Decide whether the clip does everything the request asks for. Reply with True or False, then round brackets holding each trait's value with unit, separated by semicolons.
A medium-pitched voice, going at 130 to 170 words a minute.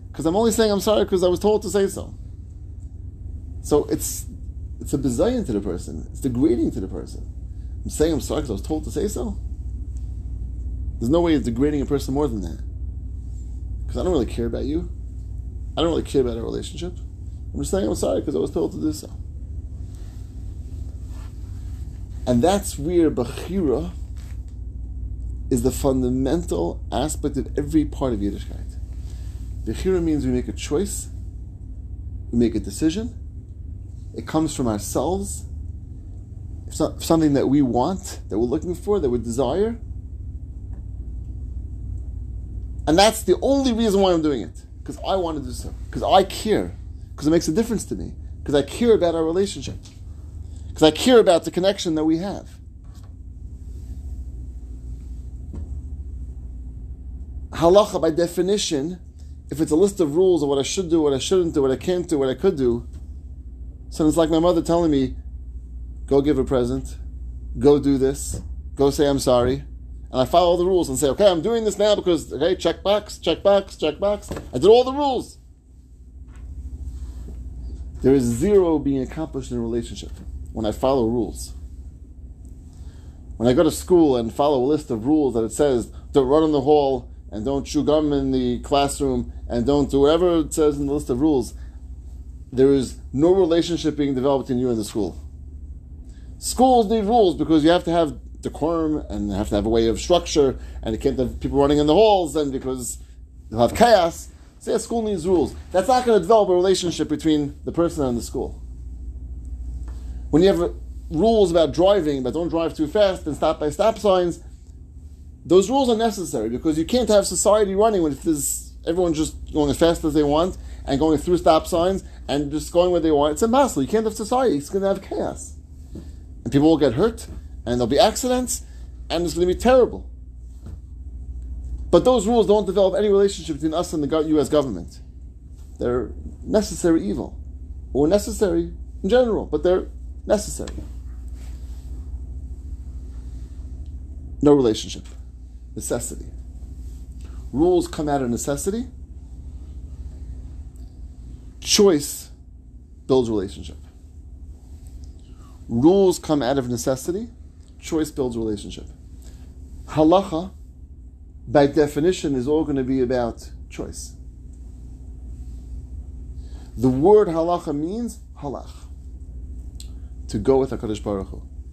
False (100 Hz; 165 wpm)